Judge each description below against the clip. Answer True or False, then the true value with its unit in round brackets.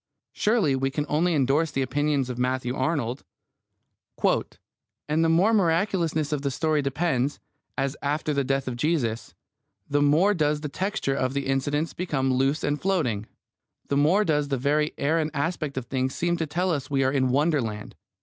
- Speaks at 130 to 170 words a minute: False (180 wpm)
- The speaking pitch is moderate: True (145 Hz)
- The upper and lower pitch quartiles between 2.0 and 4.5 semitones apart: True (3.3 semitones)